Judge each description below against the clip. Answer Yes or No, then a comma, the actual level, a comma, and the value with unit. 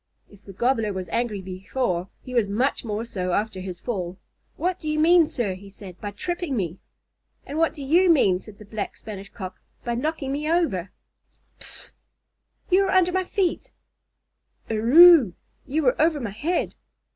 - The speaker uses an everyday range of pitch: No, wide, 8.2 semitones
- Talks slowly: No, average, 175 wpm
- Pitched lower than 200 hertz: No, high, 235 Hz